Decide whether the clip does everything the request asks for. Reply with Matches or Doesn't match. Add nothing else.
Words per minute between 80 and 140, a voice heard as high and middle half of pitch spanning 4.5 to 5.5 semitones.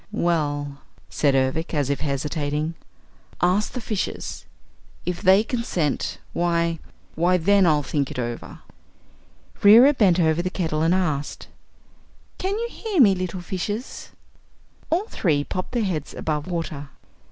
Doesn't match